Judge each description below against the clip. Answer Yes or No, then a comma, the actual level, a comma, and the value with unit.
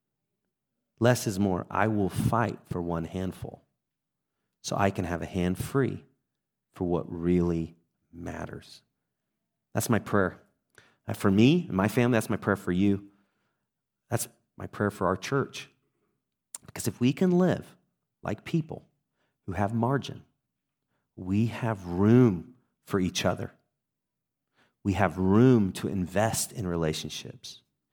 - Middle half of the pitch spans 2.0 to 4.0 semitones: No, wide, 5.4 semitones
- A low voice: Yes, low, 100 Hz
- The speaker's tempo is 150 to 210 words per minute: No, slow, 135 wpm